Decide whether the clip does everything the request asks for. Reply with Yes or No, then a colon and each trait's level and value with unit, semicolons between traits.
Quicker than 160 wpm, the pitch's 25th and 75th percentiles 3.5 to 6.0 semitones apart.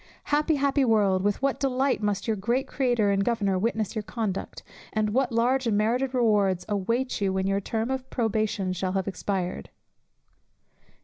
Yes: average, 170 wpm; average, 4.2 semitones